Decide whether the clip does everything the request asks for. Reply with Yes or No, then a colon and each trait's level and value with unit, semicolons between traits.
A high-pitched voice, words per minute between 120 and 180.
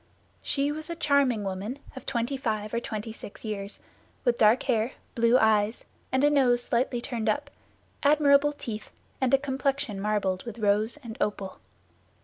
Yes: high, 235 Hz; average, 160 wpm